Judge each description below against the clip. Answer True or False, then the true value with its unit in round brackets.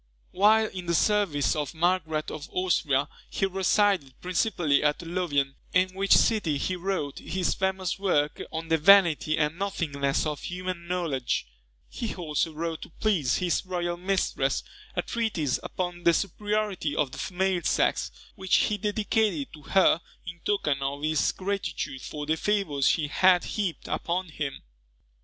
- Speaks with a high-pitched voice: False (175 Hz)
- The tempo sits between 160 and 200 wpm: False (150 wpm)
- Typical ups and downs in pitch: True (4.1 semitones)